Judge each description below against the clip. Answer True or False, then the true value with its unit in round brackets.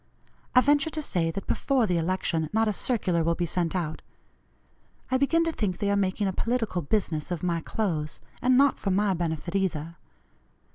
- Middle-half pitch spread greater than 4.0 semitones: True (5.0 semitones)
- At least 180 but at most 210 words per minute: True (190 wpm)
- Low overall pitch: False (190 Hz)